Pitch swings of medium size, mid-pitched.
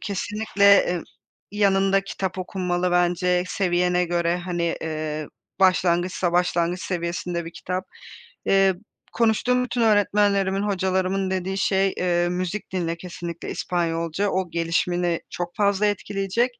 No: narrow, 2.1 semitones; medium, 180 Hz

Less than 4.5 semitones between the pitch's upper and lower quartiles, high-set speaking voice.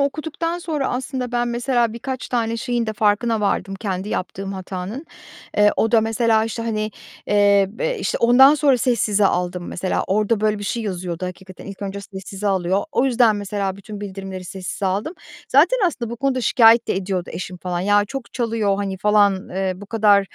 Yes: average, 3.5 semitones; high, 210 Hz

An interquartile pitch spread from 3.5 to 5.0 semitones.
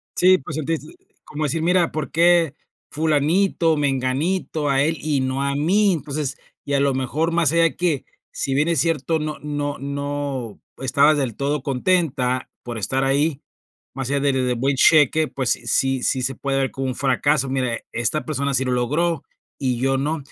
No: average, 2.9 semitones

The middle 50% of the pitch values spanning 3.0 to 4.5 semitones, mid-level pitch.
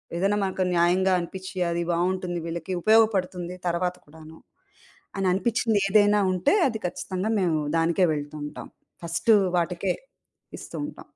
No: narrow, 2.4 semitones; medium, 180 Hz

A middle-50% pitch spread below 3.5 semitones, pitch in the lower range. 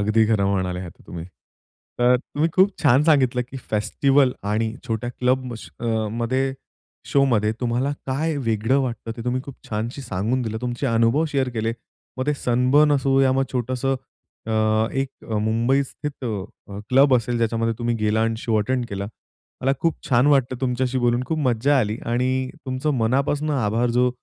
Yes: average, 3.1 semitones; low, 125 Hz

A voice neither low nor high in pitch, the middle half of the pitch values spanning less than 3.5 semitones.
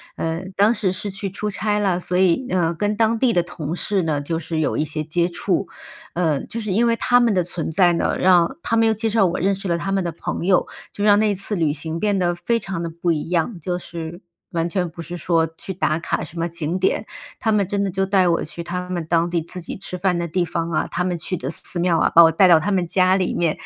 Yes: medium, 180 Hz; average, 2.7 semitones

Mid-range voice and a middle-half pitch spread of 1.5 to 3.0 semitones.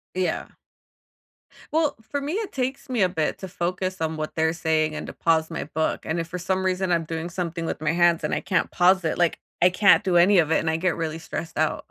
Yes: medium, 175 Hz; narrow, 2.6 semitones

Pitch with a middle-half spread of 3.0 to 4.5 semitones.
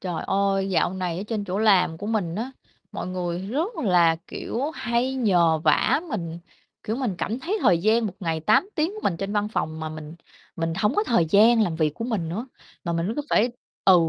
No: average, 5.1 semitones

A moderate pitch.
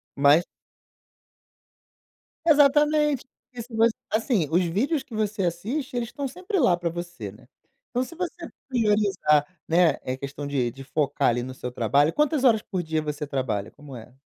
Yes: medium, 180 Hz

